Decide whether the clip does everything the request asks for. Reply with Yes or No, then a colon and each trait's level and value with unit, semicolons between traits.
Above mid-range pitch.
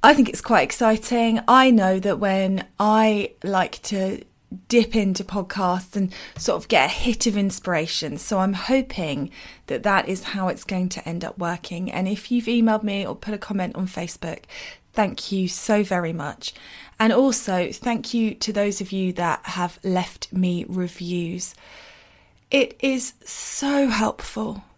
Yes: high, 200 Hz